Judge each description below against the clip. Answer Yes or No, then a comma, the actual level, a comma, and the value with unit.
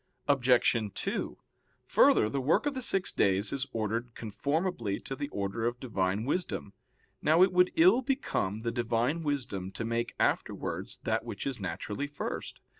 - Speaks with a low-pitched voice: Yes, low, 120 Hz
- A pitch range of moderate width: No, wide, 5.9 semitones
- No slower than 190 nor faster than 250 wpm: No, average, 160 wpm